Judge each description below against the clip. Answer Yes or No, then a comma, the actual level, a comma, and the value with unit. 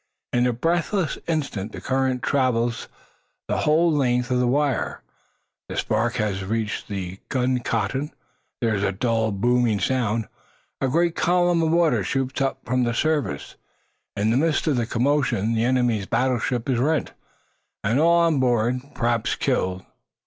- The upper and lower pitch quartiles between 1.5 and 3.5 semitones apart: No, average, 4.1 semitones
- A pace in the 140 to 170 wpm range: Yes, average, 155 wpm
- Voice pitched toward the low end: Yes, low, 125 Hz